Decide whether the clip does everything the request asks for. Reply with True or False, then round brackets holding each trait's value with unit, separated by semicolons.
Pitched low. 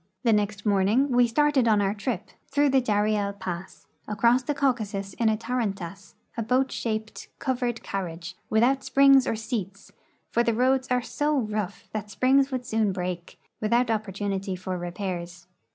False (215 Hz)